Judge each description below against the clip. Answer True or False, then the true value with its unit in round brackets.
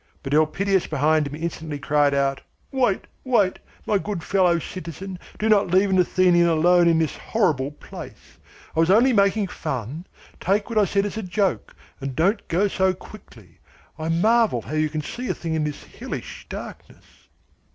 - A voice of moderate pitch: True (175 Hz)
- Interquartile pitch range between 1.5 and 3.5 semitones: False (4.5 semitones)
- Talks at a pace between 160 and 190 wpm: True (175 wpm)